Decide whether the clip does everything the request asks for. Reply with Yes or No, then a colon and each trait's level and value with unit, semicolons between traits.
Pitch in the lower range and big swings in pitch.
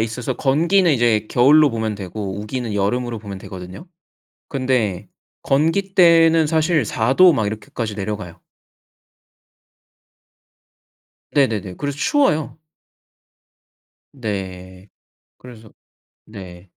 Yes: low, 115 Hz; wide, 6.8 semitones